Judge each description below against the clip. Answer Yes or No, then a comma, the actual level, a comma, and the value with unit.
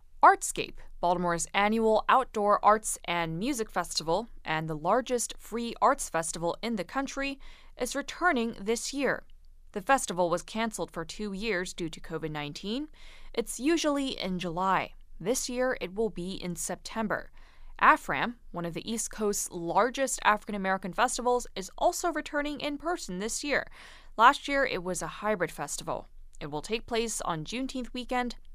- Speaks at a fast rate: No, average, 155 wpm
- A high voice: Yes, high, 215 Hz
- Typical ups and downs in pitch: No, wide, 6.4 semitones